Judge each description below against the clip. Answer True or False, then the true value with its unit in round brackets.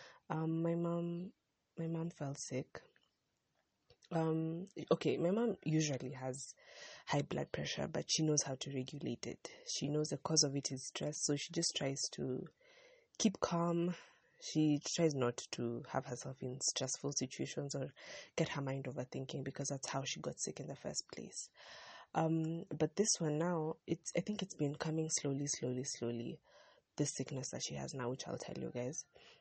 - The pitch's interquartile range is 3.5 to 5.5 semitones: True (3.8 semitones)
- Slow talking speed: False (180 wpm)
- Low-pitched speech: False (155 Hz)